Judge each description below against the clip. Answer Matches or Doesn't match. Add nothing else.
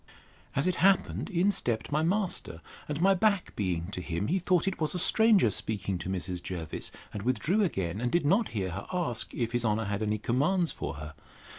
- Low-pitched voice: Matches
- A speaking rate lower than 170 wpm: Doesn't match